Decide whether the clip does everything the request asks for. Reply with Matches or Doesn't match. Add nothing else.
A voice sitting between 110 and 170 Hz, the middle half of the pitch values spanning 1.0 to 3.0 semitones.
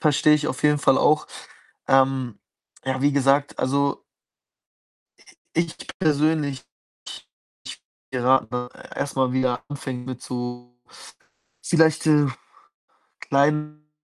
Matches